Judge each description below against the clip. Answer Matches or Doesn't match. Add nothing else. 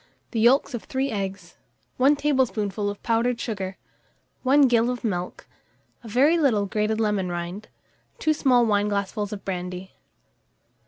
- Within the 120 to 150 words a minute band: Matches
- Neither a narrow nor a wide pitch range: Matches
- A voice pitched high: Matches